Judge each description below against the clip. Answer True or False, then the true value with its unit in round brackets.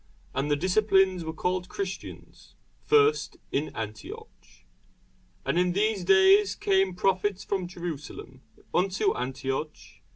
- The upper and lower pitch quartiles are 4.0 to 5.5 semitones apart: False (3.4 semitones)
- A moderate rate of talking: False (110 wpm)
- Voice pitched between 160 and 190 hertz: True (185 Hz)